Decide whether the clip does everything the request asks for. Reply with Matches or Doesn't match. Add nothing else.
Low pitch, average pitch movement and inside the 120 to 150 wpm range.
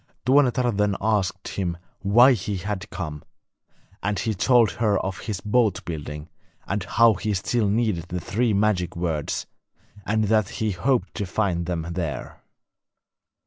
Matches